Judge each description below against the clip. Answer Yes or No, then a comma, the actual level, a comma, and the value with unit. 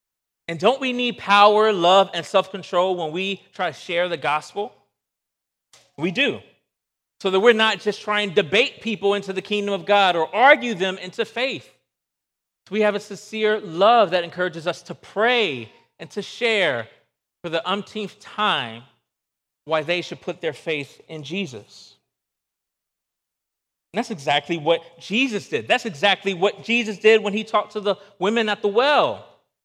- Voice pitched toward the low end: No, high, 200 Hz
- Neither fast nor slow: Yes, average, 165 wpm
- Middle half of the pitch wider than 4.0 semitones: No, average, 3.6 semitones